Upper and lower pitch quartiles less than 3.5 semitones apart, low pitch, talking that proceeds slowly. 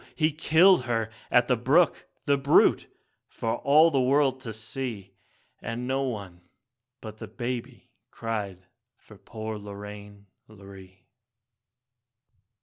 No: average, 4.7 semitones; low, 115 Hz; slow, 120 wpm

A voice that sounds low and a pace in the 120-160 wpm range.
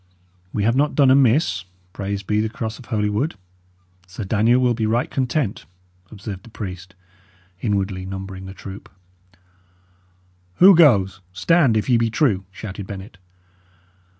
Yes: low, 110 Hz; average, 145 wpm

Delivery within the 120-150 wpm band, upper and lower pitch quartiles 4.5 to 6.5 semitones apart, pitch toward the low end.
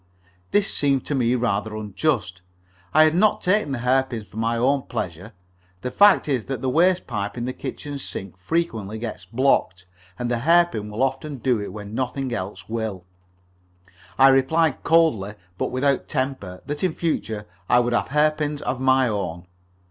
No: average, 170 wpm; average, 5.2 semitones; low, 125 Hz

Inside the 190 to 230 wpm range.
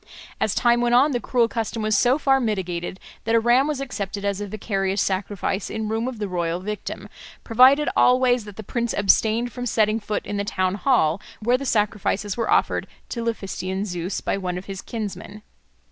Yes: average, 195 wpm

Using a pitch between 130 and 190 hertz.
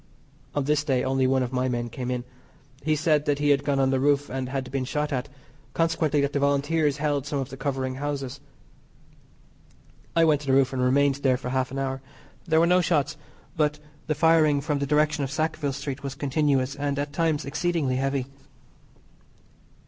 Yes: medium, 140 Hz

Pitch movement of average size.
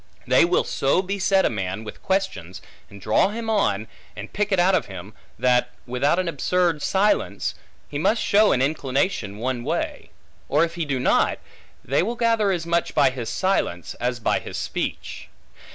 No: wide, 8.0 semitones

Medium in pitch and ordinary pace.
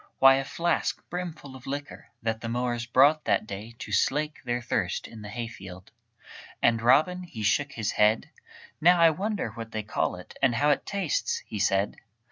No: low, 120 Hz; average, 185 wpm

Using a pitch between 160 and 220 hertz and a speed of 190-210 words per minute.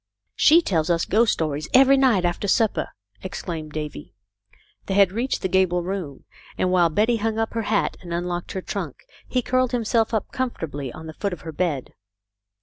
Yes: high, 190 Hz; average, 195 wpm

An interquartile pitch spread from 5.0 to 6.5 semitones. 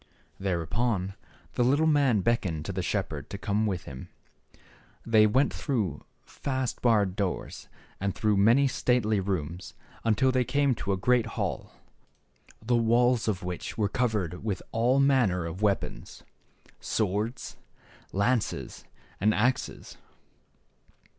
No: average, 4.5 semitones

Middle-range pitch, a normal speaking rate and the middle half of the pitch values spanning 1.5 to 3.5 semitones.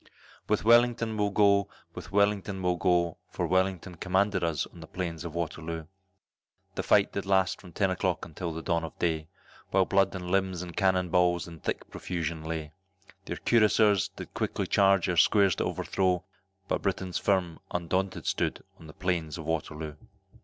No: very low, 90 Hz; average, 175 wpm; average, 2.8 semitones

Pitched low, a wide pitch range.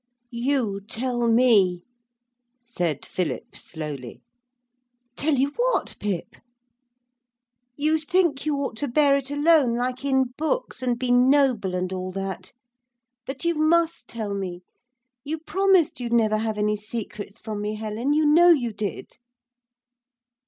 No: high, 245 Hz; wide, 5.8 semitones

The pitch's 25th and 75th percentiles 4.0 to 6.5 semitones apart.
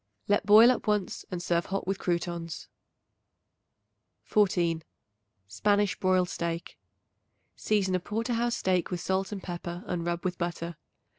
No: average, 3.1 semitones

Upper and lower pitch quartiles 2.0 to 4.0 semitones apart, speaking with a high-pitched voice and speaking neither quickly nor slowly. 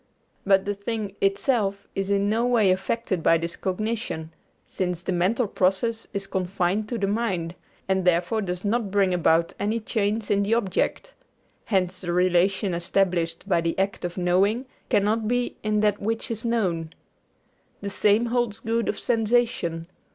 Yes: average, 3.6 semitones; high, 200 Hz; average, 160 wpm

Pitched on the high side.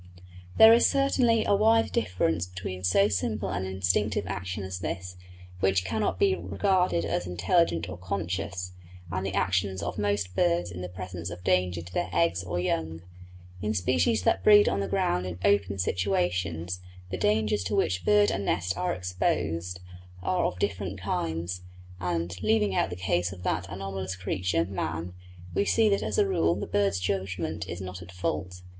No: very low, 90 Hz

